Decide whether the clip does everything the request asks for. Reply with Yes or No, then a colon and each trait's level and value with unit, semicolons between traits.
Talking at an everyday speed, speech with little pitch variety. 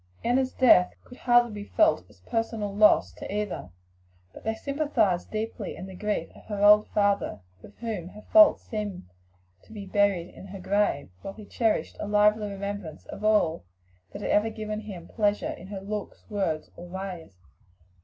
Yes: average, 180 wpm; narrow, 2.1 semitones